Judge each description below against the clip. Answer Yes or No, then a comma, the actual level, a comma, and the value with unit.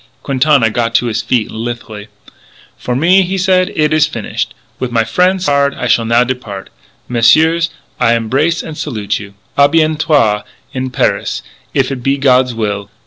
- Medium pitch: No, low, 130 Hz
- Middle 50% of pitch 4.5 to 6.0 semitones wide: Yes, average, 5.2 semitones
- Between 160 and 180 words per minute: Yes, average, 165 wpm